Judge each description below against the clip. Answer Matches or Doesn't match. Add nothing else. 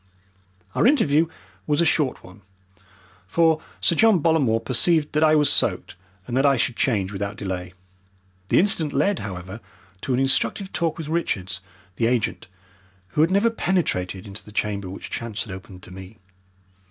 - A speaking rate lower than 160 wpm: Doesn't match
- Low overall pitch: Matches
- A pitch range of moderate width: Doesn't match